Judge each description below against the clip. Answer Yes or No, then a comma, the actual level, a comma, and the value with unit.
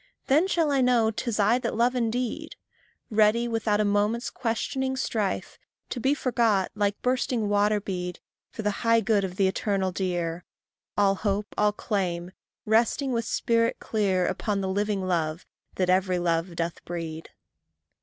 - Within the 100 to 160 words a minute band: Yes, average, 155 wpm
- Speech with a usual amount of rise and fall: Yes, average, 3.7 semitones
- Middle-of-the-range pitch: No, high, 210 Hz